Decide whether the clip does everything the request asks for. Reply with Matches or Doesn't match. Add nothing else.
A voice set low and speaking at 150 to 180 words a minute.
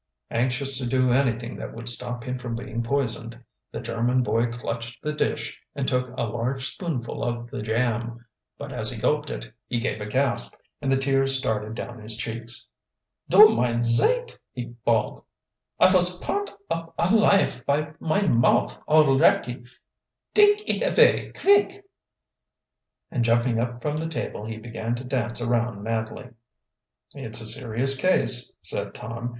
Matches